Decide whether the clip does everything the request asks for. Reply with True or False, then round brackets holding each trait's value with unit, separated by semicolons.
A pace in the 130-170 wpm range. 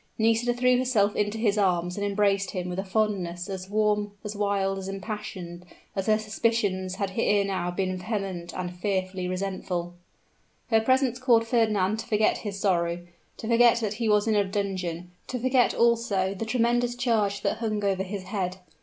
False (180 wpm)